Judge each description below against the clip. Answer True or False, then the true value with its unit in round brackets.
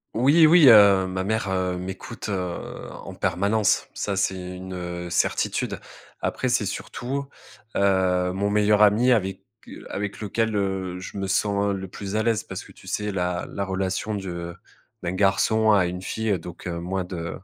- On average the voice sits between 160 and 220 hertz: False (95 Hz)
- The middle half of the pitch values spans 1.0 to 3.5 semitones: True (2.4 semitones)